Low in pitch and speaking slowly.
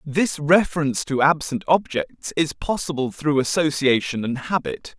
No: medium, 150 Hz; slow, 130 wpm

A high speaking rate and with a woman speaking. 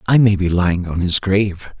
No: fast, 235 wpm; male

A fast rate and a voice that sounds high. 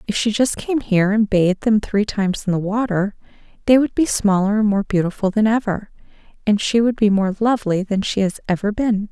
Yes: fast, 215 wpm; high, 210 Hz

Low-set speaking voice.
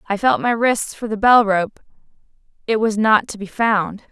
No: high, 215 Hz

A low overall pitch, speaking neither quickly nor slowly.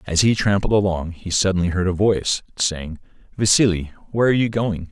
Yes: very low, 95 Hz; average, 185 wpm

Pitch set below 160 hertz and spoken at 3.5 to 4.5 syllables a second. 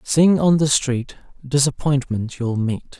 Yes: low, 135 Hz; 3.8 syllables/s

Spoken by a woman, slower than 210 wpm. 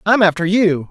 No: male; average, 200 wpm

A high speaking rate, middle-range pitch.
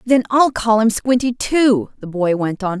No: fast, 215 wpm; high, 225 Hz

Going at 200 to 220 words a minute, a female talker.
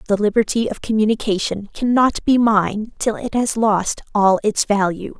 No: average, 160 wpm; female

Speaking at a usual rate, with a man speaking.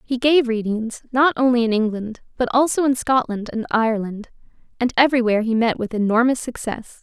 No: average, 170 wpm; female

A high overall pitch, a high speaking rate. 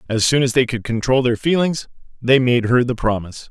No: low, 125 Hz; fast, 220 wpm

